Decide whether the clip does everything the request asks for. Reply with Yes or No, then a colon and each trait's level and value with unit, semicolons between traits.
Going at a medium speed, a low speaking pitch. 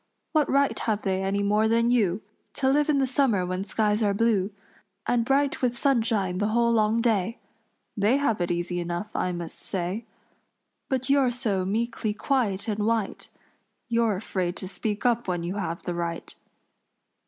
No: average, 175 wpm; high, 215 Hz